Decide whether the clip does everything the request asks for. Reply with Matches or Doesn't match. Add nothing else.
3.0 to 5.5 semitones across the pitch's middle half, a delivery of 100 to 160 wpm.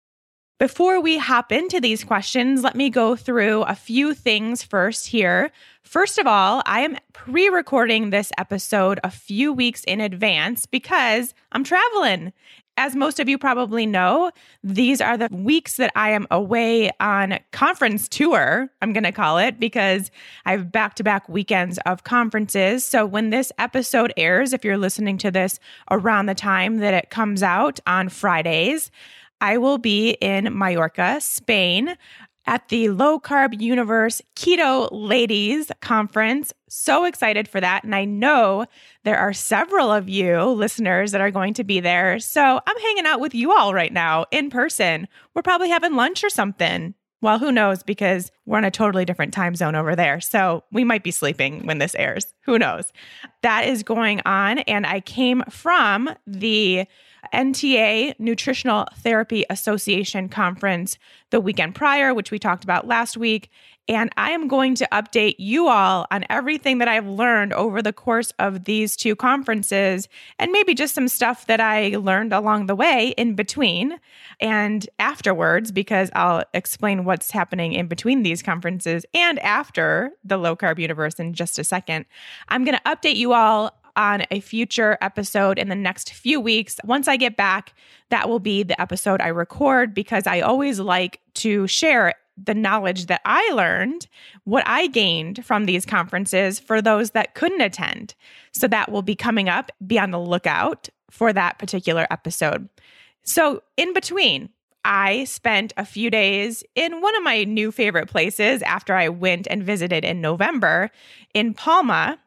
Doesn't match